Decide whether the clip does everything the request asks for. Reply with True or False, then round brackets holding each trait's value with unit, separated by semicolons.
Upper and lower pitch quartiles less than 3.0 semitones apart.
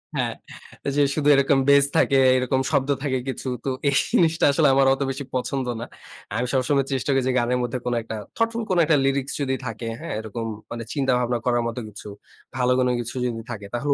True (2.5 semitones)